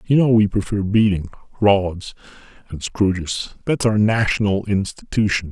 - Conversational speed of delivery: No, slow, 110 wpm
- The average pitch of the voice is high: No, low, 100 Hz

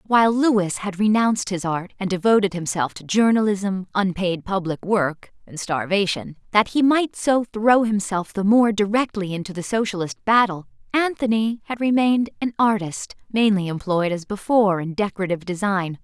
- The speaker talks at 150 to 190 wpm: Yes, average, 155 wpm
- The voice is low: No, high, 200 Hz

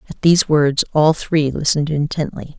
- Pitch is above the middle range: No, medium, 150 Hz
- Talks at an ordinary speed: Yes, average, 160 wpm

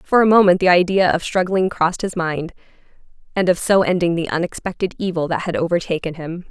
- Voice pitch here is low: No, medium, 175 Hz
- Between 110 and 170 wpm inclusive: No, average, 195 wpm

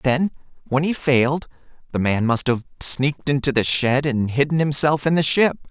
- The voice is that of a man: Yes, male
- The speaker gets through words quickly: No, average, 190 wpm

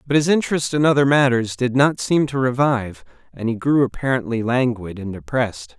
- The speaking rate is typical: Yes, average, 185 wpm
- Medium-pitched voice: No, low, 125 Hz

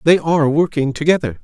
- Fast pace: No, average, 170 wpm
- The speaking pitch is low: No, medium, 155 Hz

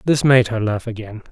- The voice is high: No, low, 115 Hz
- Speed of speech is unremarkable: No, fast, 230 wpm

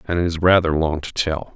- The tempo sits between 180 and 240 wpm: No, fast, 270 wpm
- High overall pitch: No, very low, 85 Hz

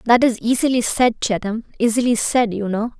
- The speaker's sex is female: Yes, female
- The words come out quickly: No, average, 180 wpm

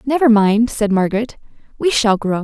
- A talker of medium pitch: No, high, 225 Hz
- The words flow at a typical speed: Yes, average, 175 wpm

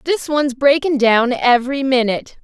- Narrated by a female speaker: Yes, female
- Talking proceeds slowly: No, average, 175 wpm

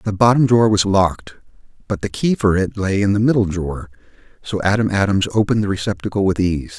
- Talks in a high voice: No, low, 100 Hz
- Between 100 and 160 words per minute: No, fast, 205 wpm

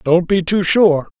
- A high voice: No, medium, 180 Hz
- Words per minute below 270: Yes, average, 200 wpm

